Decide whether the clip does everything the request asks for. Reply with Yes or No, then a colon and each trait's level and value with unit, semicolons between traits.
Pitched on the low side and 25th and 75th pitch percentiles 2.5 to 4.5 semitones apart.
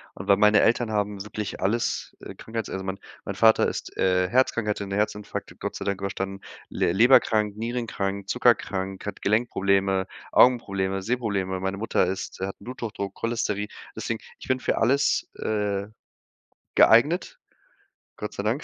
Yes: low, 105 Hz; average, 2.8 semitones